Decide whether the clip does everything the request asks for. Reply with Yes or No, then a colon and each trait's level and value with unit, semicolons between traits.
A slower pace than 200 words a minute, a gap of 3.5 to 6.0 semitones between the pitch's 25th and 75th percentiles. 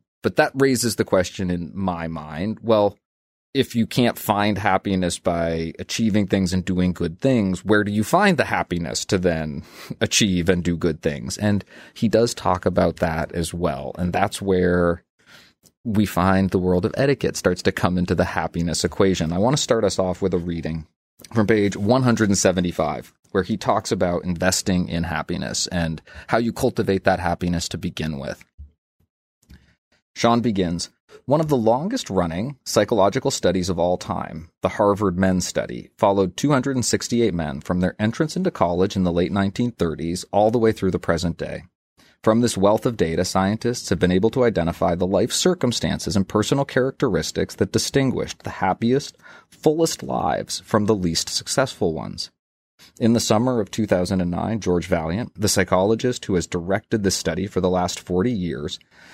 Yes: average, 170 wpm; average, 4.1 semitones